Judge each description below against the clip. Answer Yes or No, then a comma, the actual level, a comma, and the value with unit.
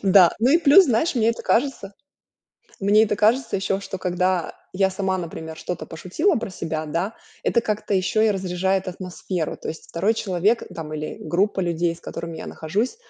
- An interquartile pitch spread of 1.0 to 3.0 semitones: No, average, 4.0 semitones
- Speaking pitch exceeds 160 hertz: Yes, high, 190 Hz